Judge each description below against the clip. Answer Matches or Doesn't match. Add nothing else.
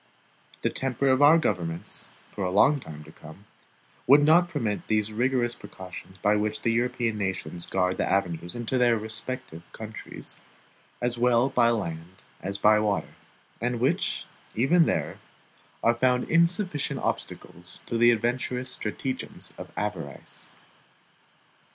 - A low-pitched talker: Matches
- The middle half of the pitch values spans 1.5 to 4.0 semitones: Doesn't match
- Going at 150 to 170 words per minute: Doesn't match